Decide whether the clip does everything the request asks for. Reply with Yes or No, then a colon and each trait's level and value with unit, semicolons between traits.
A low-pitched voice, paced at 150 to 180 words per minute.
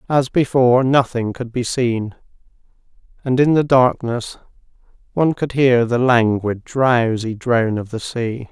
No: low, 125 Hz; average, 140 wpm